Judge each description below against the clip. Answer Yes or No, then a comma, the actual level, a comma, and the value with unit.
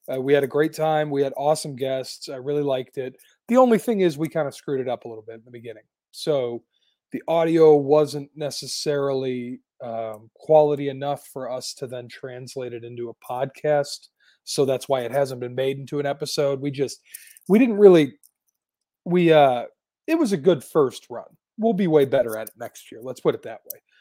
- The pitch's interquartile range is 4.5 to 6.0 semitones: No, average, 3.2 semitones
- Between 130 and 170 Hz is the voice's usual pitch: Yes, medium, 140 Hz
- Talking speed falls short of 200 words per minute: No, fast, 205 wpm